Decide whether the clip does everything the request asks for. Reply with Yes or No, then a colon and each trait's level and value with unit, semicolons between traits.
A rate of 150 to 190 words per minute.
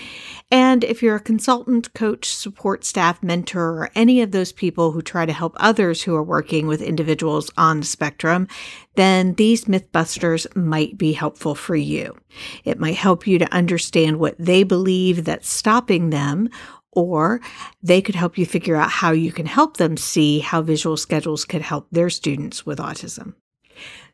Yes: average, 170 wpm